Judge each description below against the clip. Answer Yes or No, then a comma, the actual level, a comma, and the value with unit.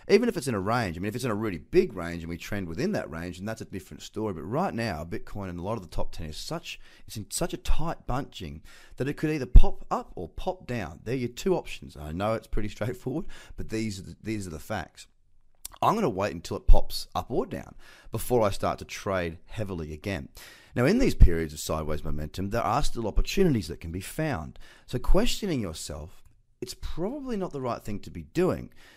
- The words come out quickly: Yes, fast, 235 wpm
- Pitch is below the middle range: Yes, low, 100 Hz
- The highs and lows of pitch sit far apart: Yes, wide, 6.1 semitones